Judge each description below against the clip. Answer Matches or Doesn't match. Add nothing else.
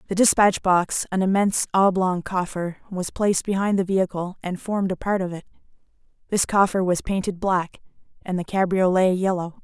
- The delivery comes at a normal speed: Matches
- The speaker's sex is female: Matches